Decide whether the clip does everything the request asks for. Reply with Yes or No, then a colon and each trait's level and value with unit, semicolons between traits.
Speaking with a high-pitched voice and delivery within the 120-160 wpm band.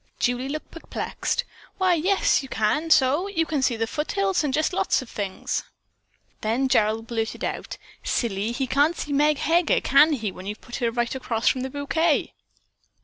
No: very high, 270 Hz; average, 180 wpm